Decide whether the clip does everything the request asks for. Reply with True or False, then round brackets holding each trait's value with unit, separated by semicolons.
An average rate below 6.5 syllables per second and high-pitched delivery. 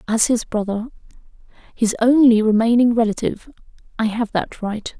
True (5.3 syllables/s; 225 Hz)